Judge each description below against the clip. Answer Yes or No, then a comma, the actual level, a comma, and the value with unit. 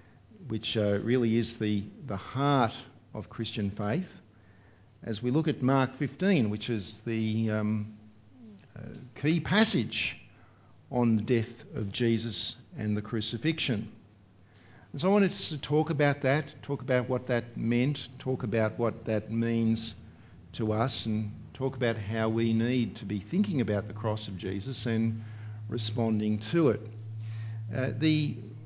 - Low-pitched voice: Yes, low, 115 Hz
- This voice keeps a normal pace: Yes, average, 150 wpm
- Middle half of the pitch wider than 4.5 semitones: No, average, 2.9 semitones